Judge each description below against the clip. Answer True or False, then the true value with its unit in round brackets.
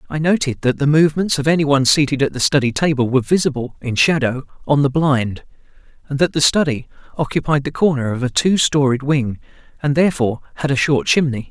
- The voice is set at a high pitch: False (140 Hz)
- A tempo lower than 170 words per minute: False (195 wpm)